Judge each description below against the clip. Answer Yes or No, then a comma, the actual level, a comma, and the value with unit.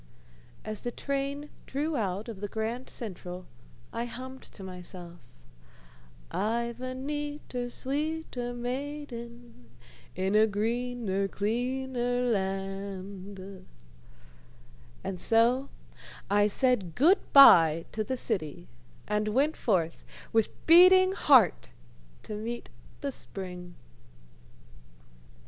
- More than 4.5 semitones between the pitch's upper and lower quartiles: Yes, average, 5.1 semitones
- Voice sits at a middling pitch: No, high, 230 Hz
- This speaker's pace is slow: Yes, slow, 100 wpm